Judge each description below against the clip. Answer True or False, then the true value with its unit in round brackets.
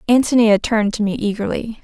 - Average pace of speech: True (165 wpm)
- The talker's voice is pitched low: False (215 Hz)